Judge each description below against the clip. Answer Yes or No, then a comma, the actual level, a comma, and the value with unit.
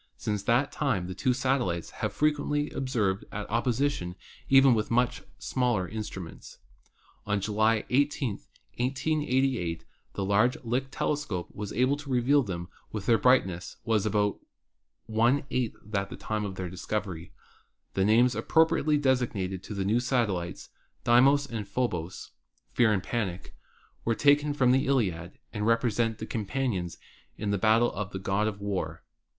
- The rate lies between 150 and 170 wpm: Yes, average, 155 wpm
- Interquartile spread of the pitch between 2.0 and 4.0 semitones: No, average, 4.7 semitones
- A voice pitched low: Yes, low, 115 Hz